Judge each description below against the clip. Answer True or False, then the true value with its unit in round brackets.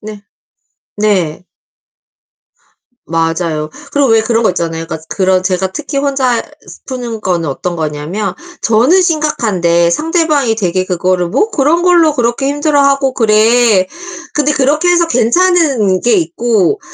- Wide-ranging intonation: True (7.9 semitones)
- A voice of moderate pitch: False (225 Hz)